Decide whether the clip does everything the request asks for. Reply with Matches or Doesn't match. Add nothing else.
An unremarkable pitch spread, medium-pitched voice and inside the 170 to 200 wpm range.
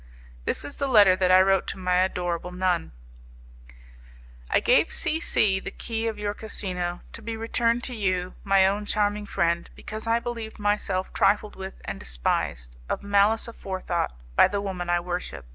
Doesn't match